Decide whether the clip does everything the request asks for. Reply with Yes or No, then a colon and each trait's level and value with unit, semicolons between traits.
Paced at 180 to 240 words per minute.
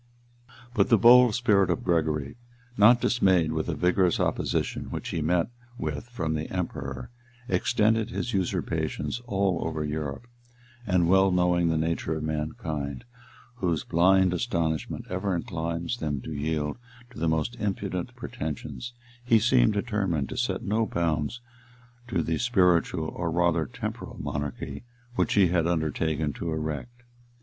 No: average, 145 wpm